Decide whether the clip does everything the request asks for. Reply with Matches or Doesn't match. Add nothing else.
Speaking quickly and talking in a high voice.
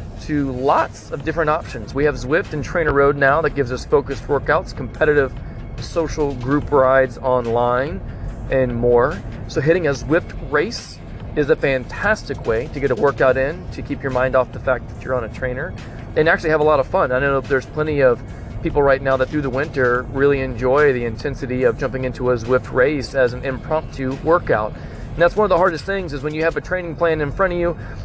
Doesn't match